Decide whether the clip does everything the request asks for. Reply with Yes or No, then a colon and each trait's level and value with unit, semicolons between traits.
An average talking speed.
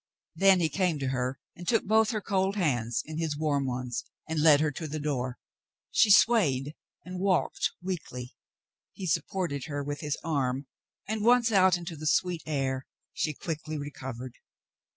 Yes: average, 170 wpm